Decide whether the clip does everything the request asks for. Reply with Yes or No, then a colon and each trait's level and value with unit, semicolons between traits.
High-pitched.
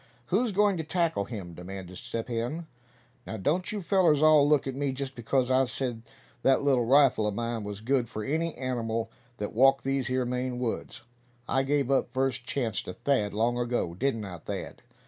No: low, 130 Hz